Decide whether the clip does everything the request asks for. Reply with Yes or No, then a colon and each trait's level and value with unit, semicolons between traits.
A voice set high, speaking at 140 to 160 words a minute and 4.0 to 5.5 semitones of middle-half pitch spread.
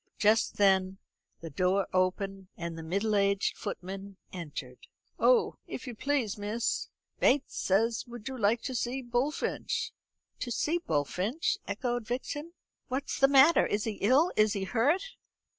Yes: high, 215 Hz; average, 145 wpm; average, 5.0 semitones